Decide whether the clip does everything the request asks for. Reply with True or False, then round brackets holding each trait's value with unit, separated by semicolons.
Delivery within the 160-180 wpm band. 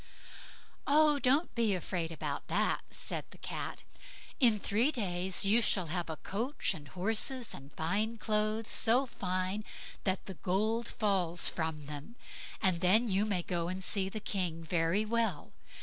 False (150 wpm)